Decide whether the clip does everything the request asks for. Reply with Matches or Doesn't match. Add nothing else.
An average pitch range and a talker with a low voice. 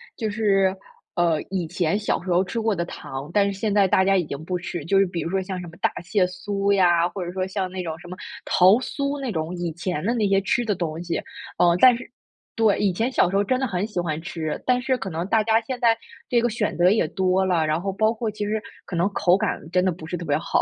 Doesn't match